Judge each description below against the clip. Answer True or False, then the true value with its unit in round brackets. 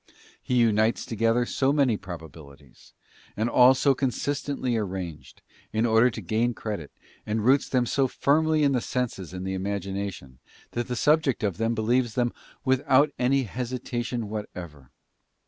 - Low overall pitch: True (115 Hz)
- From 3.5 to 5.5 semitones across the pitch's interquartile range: True (4.4 semitones)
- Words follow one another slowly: False (150 wpm)